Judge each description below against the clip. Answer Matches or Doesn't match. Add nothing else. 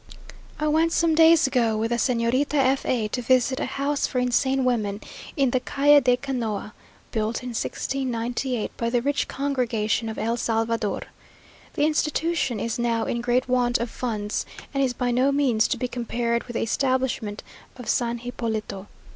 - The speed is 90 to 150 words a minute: Doesn't match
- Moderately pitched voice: Doesn't match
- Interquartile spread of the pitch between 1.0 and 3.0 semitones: Matches